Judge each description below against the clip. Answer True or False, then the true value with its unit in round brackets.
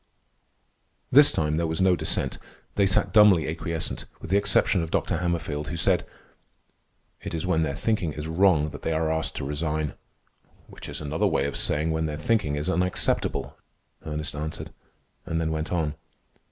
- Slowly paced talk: False (175 wpm)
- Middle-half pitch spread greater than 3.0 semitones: False (2.4 semitones)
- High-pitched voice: False (80 Hz)